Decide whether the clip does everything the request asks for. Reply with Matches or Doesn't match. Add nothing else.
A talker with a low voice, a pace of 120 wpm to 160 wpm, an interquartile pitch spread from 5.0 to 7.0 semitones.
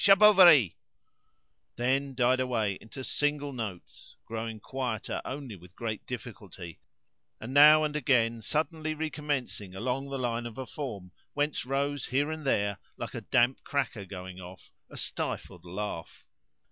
Matches